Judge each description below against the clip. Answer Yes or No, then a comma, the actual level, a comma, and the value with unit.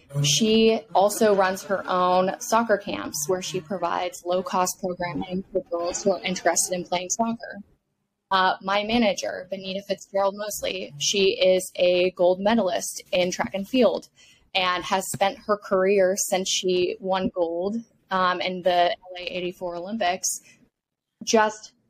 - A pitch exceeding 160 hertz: Yes, high, 190 Hz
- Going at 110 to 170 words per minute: Yes, average, 140 wpm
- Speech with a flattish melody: Yes, narrow, 1.9 semitones